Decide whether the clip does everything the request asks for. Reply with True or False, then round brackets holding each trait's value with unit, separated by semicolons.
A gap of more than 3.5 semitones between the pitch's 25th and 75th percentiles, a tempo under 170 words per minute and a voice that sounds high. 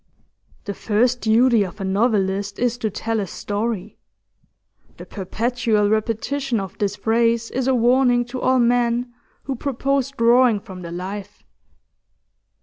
False (3.2 semitones; 140 wpm; 230 Hz)